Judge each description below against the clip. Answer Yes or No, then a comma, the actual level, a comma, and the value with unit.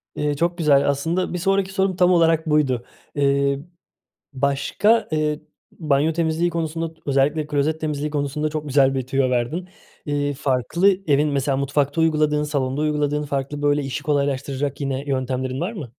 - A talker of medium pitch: Yes, medium, 145 Hz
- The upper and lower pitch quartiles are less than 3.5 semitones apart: Yes, narrow, 2.6 semitones